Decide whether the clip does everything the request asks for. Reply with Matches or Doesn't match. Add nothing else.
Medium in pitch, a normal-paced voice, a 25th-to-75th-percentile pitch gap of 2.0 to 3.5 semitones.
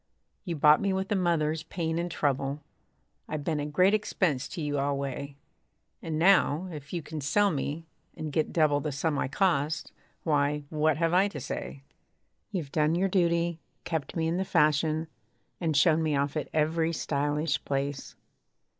Matches